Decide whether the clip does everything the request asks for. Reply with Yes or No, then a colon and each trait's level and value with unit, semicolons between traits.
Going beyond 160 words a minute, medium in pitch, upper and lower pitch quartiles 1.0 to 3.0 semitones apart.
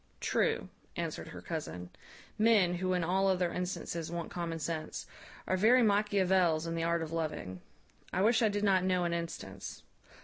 Yes: average, 170 wpm; medium, 180 Hz; narrow, 2.6 semitones